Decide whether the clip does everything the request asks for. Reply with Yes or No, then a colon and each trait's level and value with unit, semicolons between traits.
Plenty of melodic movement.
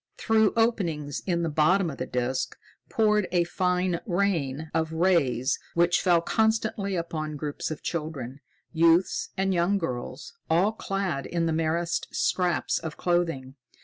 No: average, 3.5 semitones